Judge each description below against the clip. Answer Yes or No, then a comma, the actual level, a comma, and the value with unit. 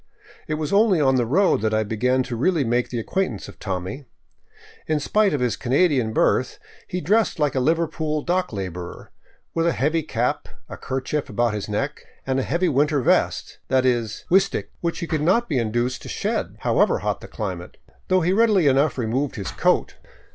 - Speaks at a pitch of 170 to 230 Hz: No, low, 135 Hz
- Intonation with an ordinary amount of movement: No, wide, 5.9 semitones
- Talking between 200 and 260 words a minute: Yes, fast, 205 wpm